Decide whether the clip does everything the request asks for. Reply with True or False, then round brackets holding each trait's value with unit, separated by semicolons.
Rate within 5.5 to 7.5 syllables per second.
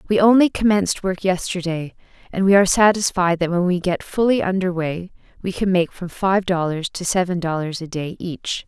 False (5.2 syllables/s)